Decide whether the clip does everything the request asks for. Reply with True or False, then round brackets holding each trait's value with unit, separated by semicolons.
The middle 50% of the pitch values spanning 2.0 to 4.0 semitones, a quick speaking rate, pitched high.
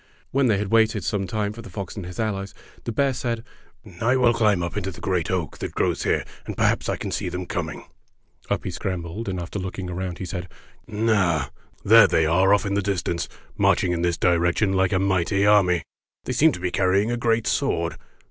False (3.5 semitones; 225 wpm; 95 Hz)